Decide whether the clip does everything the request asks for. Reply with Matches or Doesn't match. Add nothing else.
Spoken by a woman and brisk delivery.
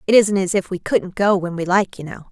Matches